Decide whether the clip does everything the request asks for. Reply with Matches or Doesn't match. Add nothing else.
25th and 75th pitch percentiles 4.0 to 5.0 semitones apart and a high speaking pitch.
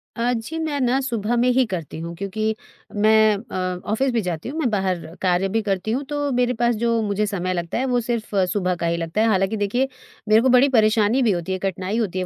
Matches